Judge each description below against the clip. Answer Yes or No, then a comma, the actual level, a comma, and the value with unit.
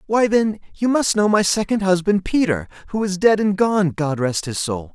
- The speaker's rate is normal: No, fast, 220 wpm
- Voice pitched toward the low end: No, high, 190 Hz